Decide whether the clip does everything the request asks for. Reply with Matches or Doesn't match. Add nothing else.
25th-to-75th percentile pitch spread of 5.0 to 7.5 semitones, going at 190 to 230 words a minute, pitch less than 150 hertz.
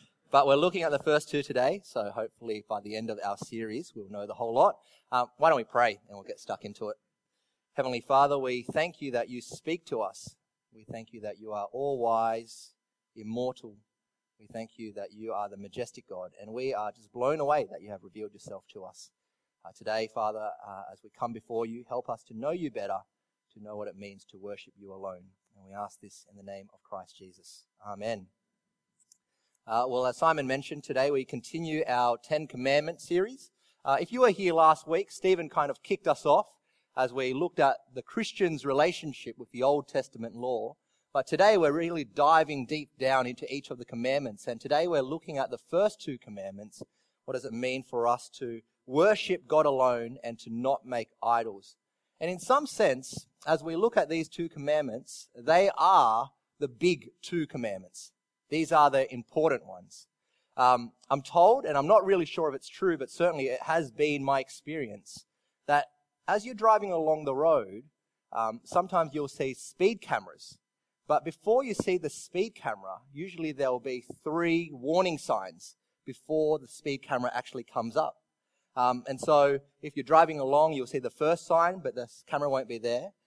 Matches